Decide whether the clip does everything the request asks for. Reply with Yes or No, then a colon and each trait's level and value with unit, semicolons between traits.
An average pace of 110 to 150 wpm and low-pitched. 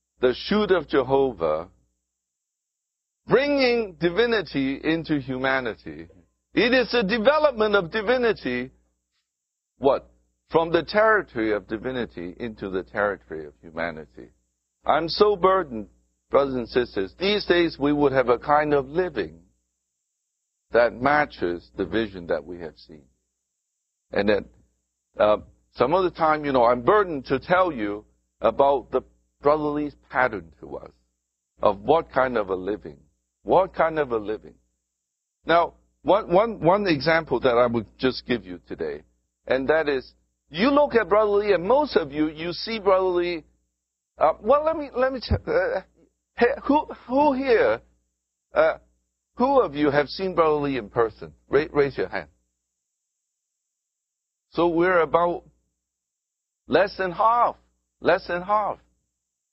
Yes: average, 140 wpm; low, 130 Hz